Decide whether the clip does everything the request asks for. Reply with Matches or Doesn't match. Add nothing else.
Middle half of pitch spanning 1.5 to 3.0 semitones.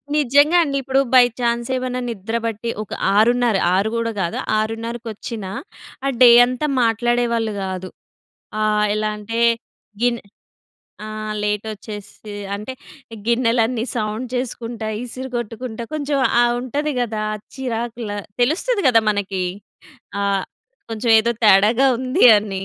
Matches